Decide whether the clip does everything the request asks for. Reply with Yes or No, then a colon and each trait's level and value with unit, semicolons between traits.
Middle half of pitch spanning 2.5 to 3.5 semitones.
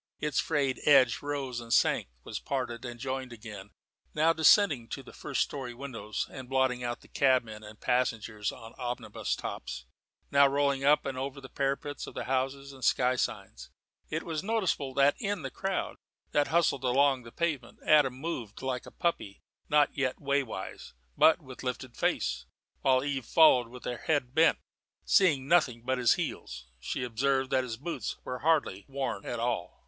Yes: average, 2.9 semitones